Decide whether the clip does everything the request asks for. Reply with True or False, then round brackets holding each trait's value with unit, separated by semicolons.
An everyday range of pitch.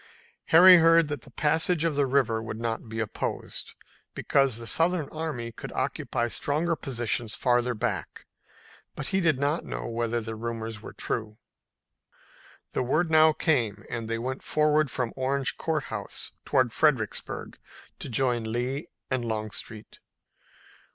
True (5.0 semitones)